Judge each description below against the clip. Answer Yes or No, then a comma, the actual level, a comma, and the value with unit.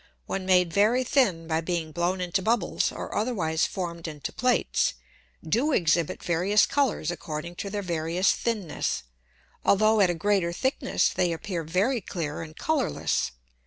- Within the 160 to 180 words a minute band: No, average, 150 wpm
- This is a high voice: No, medium, 180 Hz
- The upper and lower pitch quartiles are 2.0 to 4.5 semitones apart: Yes, average, 4.2 semitones